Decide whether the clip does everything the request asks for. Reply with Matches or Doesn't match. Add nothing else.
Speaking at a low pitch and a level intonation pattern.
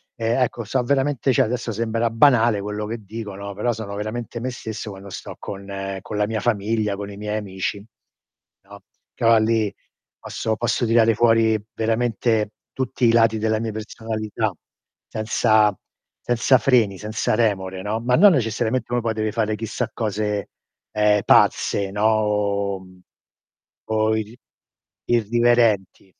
Matches